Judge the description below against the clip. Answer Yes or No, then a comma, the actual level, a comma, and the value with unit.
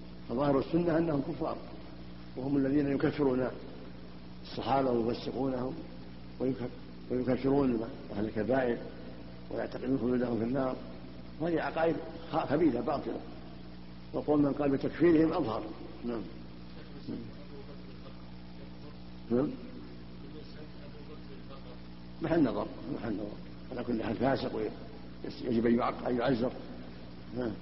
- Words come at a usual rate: Yes, average, 85 wpm